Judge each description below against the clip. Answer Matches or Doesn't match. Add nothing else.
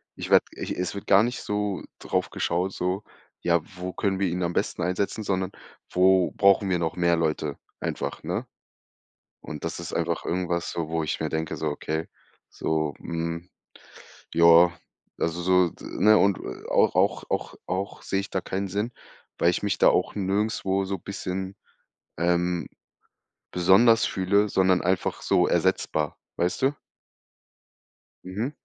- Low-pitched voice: Matches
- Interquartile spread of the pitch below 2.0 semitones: Doesn't match